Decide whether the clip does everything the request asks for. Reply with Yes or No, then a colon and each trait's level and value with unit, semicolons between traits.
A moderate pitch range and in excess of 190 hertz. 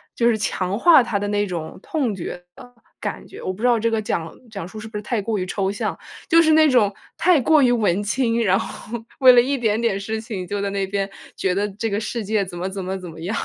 Yes: average, 3.5 semitones; high, 210 Hz